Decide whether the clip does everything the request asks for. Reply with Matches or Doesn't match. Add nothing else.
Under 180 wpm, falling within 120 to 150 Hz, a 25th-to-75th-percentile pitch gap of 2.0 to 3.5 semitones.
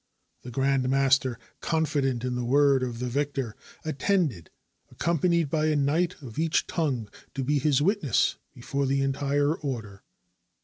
Matches